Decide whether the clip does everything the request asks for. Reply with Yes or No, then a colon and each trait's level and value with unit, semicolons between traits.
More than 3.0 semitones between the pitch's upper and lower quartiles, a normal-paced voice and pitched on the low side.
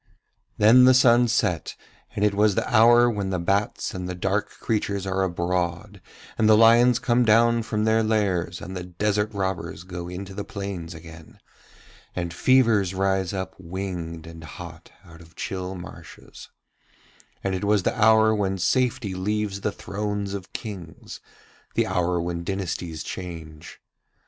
Yes: average, 3.4 semitones; average, 155 wpm; very low, 95 Hz